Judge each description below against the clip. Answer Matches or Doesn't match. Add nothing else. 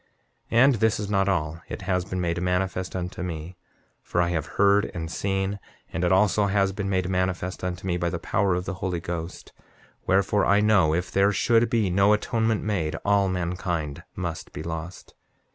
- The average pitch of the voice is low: Matches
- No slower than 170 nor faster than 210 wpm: Matches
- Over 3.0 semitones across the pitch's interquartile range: Doesn't match